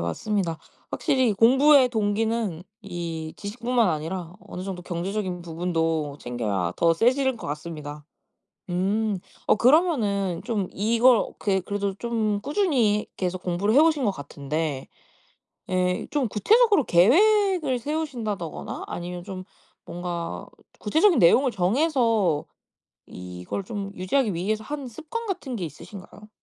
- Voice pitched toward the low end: No, high, 200 Hz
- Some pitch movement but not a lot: No, wide, 6.3 semitones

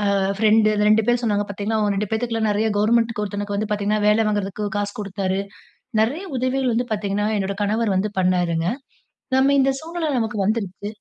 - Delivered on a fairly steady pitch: Yes, narrow, 2.0 semitones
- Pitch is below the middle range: No, high, 210 Hz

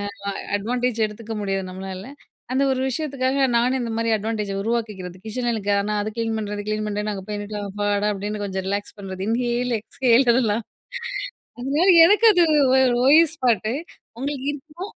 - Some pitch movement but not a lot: Yes, average, 3.8 semitones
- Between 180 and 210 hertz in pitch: No, high, 225 Hz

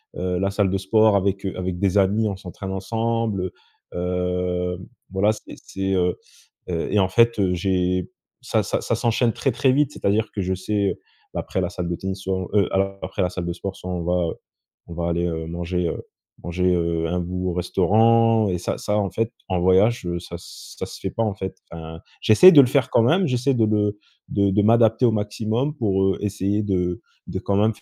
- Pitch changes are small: No, average, 3.2 semitones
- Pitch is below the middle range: Yes, very low, 95 Hz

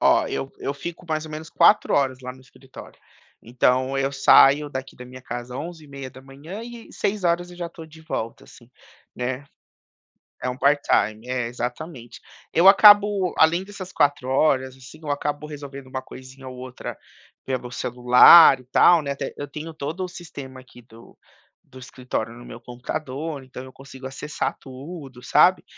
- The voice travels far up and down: No, average, 3.7 semitones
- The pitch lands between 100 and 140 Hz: Yes, low, 135 Hz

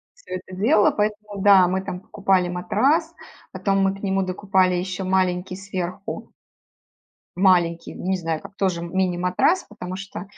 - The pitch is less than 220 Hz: Yes, high, 190 Hz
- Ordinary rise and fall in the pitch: No, narrow, 1.7 semitones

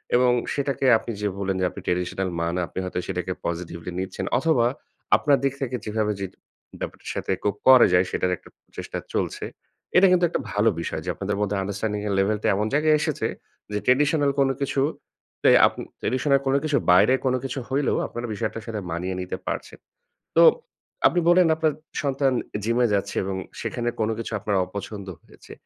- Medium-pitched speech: No, low, 110 Hz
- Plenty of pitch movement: Yes, wide, 5.9 semitones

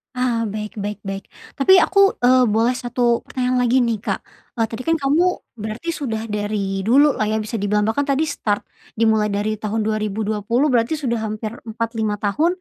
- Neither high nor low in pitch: No, high, 225 Hz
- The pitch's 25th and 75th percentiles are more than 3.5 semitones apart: No, average, 3.2 semitones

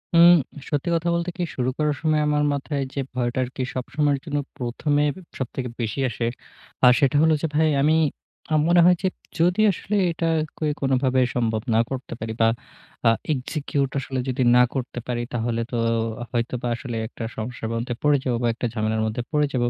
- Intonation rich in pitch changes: No, average, 3.8 semitones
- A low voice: Yes, low, 130 Hz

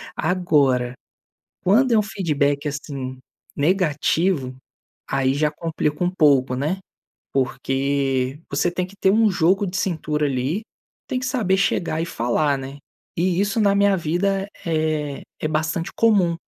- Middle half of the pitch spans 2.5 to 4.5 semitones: No, average, 5.1 semitones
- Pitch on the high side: No, medium, 155 Hz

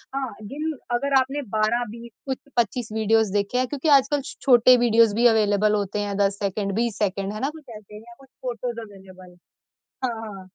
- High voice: Yes, high, 225 Hz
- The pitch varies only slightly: No, average, 3.7 semitones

